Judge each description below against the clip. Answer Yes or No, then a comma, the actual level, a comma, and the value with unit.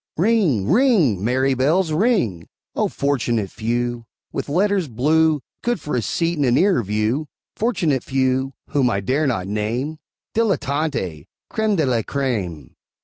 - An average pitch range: No, wide, 6.1 semitones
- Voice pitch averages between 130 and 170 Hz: Yes, low, 135 Hz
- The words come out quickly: No, average, 145 wpm